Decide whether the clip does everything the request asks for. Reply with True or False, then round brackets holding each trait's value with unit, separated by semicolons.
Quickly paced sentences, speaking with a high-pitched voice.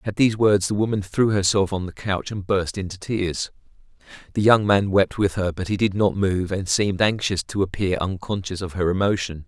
False (215 wpm; 95 Hz)